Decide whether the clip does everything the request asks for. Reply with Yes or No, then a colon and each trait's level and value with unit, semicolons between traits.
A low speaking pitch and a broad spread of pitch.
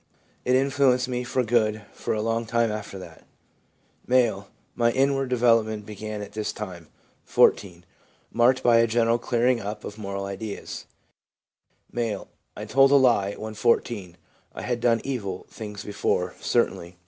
No: low, 115 Hz; average, 3.0 semitones